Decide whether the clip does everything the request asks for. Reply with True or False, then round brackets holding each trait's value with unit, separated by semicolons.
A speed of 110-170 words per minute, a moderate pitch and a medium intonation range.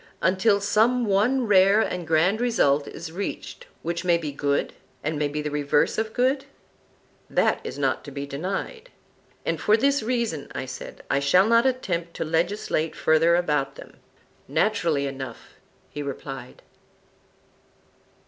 False (150 wpm; 175 Hz; 6.7 semitones)